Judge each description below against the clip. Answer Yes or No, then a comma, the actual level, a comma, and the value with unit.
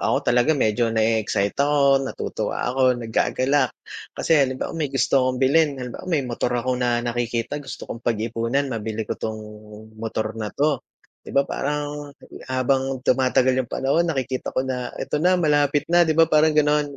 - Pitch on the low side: Yes, low, 130 Hz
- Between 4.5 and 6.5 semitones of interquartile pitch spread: No, average, 3.4 semitones